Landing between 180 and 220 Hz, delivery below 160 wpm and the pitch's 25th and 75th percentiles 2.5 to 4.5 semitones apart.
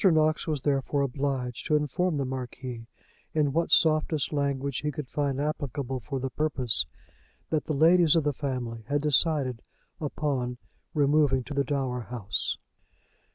No: medium, 140 Hz; average, 150 wpm; average, 2.9 semitones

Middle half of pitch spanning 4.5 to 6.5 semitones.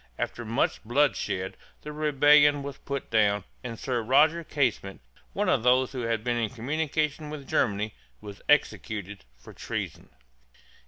Yes: average, 5.1 semitones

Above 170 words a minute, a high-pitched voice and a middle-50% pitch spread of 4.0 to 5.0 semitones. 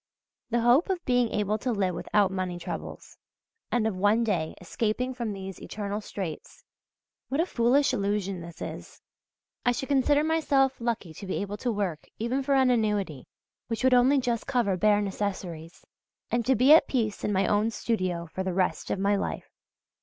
Yes: average, 185 wpm; high, 215 Hz; average, 4.4 semitones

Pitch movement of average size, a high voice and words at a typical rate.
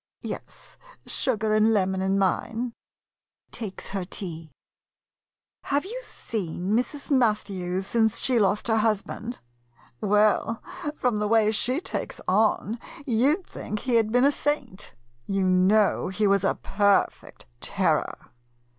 No: average, 3.4 semitones; high, 215 Hz; slow, 130 wpm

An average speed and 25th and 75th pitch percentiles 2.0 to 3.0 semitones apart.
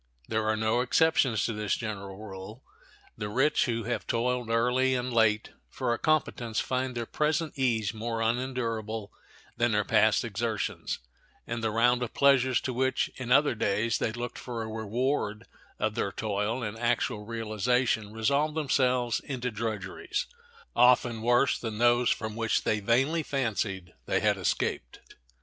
Yes: average, 155 wpm; narrow, 2.5 semitones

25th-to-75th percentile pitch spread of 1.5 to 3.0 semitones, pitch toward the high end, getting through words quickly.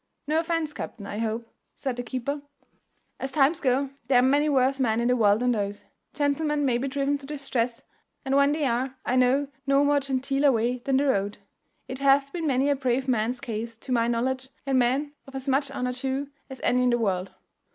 Yes: narrow, 2.5 semitones; very high, 265 Hz; fast, 215 wpm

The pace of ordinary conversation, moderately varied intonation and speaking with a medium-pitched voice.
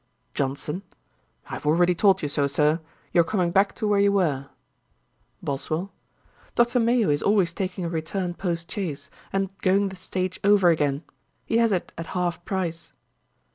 Yes: average, 170 wpm; average, 3.7 semitones; medium, 180 Hz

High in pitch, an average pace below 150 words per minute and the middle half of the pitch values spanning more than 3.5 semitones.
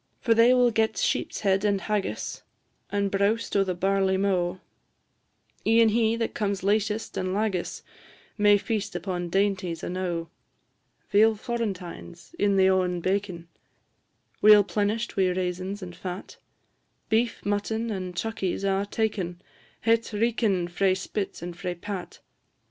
No: high, 200 Hz; slow, 135 wpm; average, 2.9 semitones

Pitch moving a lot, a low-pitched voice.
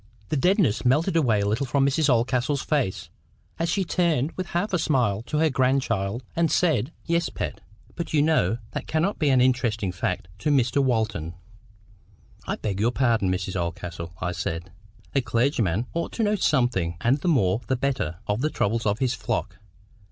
Yes: wide, 6.9 semitones; low, 125 Hz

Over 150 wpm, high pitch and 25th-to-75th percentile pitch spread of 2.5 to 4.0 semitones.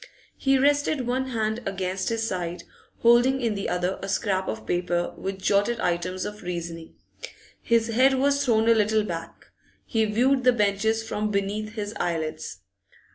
No: average, 160 wpm; high, 210 Hz; average, 4.4 semitones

